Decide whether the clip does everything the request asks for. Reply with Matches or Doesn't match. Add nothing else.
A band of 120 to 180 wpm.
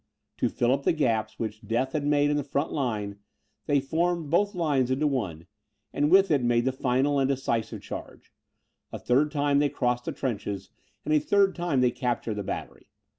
Doesn't match